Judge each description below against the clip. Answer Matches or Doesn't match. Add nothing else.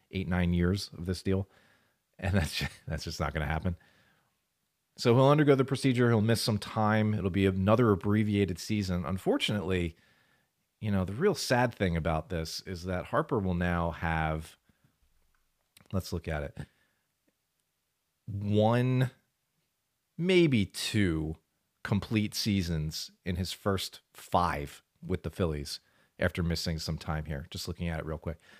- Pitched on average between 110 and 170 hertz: Doesn't match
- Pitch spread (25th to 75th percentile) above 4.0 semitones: Matches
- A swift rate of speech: Doesn't match